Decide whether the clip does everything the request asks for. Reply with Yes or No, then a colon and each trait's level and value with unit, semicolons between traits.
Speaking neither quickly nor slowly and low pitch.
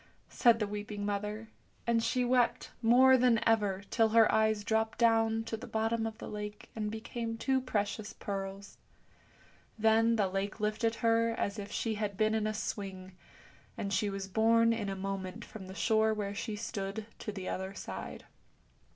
No: average, 175 wpm; high, 220 Hz